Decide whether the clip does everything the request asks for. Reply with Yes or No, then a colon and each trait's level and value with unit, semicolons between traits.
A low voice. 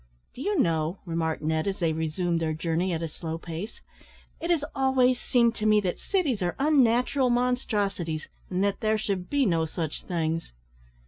No: high, 190 Hz